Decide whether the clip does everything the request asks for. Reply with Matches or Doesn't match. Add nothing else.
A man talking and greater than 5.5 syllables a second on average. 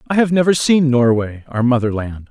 Doesn't match